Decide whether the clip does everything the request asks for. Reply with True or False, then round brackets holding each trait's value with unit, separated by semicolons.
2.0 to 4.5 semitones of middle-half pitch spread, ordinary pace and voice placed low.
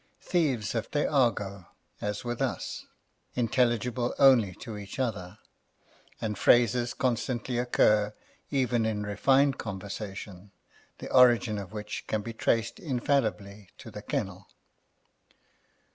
False (3.3 semitones; 115 wpm; 115 Hz)